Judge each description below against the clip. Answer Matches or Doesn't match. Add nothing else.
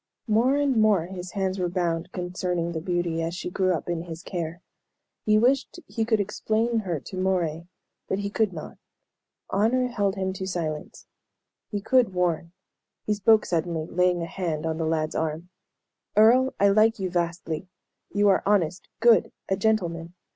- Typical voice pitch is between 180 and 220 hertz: Matches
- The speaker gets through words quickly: Doesn't match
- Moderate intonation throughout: Matches